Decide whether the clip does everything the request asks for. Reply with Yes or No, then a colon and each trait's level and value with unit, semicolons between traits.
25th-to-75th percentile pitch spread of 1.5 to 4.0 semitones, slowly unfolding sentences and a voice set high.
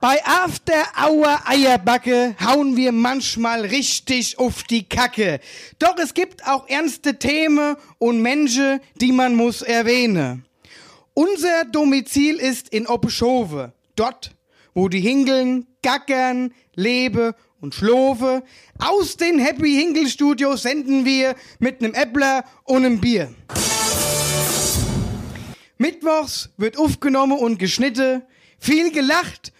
Yes: average, 3.6 semitones; slow, 105 wpm; very high, 255 Hz